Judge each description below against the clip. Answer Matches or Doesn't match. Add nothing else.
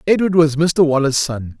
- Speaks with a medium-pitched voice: Matches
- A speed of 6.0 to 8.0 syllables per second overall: Doesn't match